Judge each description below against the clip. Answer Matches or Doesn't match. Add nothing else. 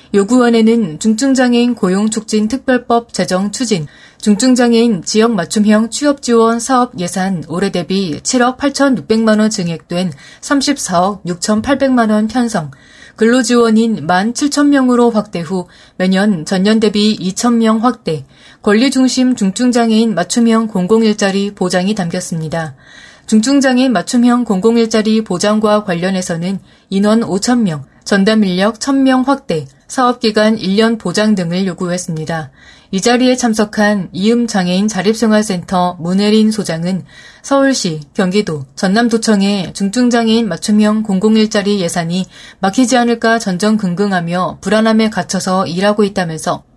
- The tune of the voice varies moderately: Matches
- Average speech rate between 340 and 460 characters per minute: Doesn't match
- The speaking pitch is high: Matches